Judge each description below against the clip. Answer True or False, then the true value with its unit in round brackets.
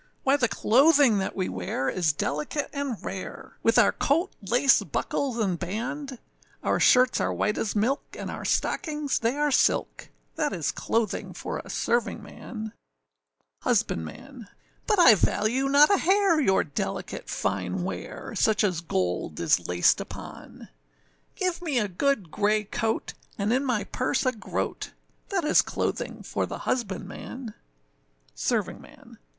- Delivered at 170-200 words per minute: False (145 wpm)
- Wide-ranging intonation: True (6.6 semitones)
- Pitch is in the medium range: False (230 Hz)